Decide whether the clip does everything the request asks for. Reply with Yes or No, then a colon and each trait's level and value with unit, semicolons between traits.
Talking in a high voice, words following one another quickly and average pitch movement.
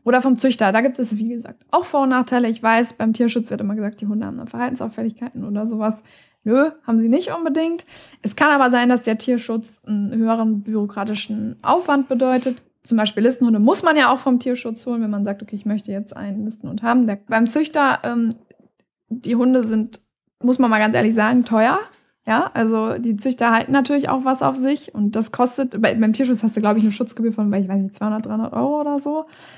Yes: high, 230 Hz; fast, 220 wpm; average, 3.0 semitones